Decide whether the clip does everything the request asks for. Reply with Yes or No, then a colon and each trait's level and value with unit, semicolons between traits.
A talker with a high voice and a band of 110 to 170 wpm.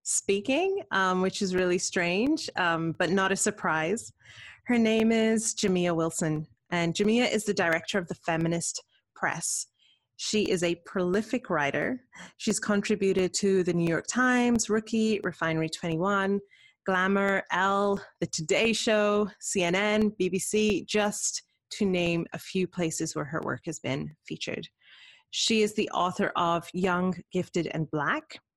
Yes: high, 195 Hz; average, 145 wpm